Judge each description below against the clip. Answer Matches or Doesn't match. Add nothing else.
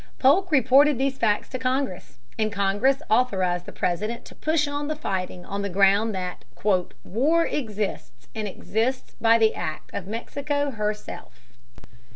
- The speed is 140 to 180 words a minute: Matches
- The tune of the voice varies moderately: Doesn't match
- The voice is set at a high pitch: Matches